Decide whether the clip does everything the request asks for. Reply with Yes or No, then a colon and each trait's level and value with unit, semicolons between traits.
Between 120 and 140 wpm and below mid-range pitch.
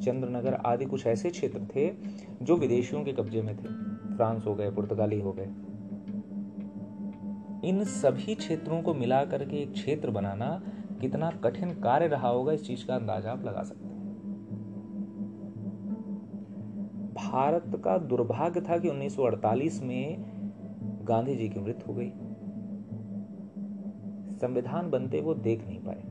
Yes: average, 135 wpm; low, 125 Hz